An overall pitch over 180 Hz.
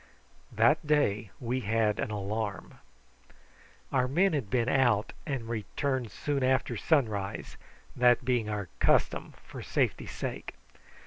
No: low, 120 Hz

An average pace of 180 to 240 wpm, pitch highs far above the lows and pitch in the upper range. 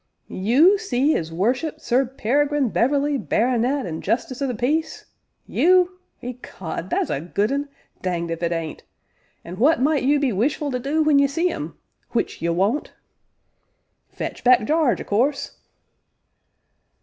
No: average, 150 wpm; wide, 6.0 semitones; very high, 255 Hz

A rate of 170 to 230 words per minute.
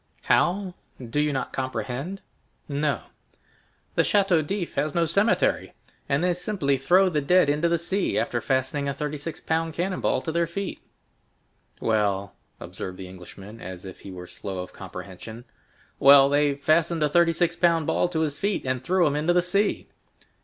Yes: average, 175 wpm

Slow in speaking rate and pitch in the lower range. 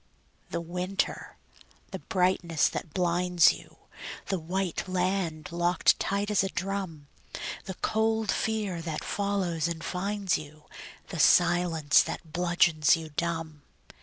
No: slow, 125 wpm; medium, 175 Hz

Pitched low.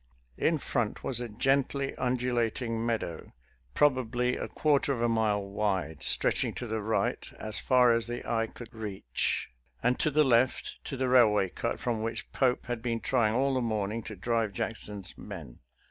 Yes: low, 115 Hz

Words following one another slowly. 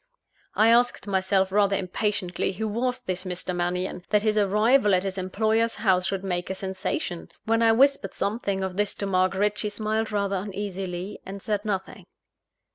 No: average, 170 wpm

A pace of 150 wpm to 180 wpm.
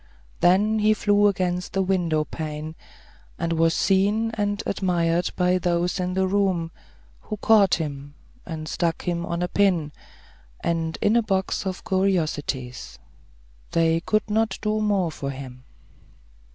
No: average, 140 wpm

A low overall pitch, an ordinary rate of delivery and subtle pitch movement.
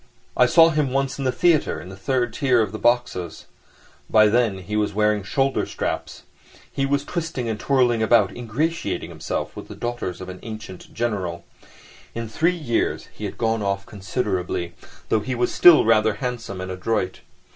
No: low, 115 Hz; average, 175 wpm; average, 4.5 semitones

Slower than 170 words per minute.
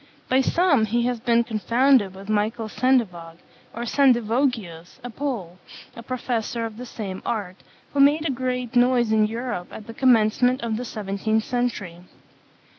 Yes: average, 155 wpm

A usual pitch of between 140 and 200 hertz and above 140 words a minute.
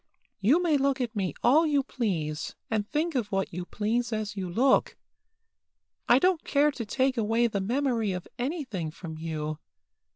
No: high, 230 Hz; average, 170 wpm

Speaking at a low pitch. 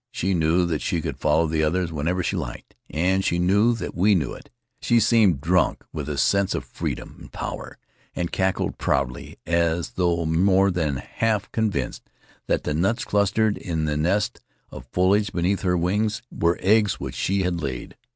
Yes: very low, 90 Hz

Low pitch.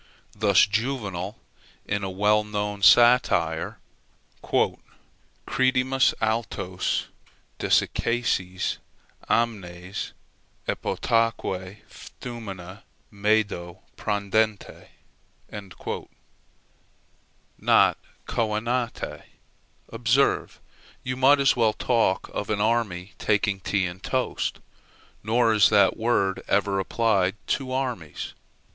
Yes: low, 105 Hz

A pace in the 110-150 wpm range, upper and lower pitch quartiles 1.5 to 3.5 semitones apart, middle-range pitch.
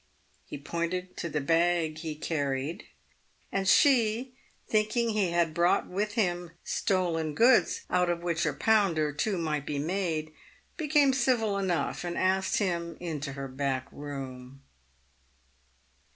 No: slow, 135 wpm; average, 4.5 semitones; medium, 175 Hz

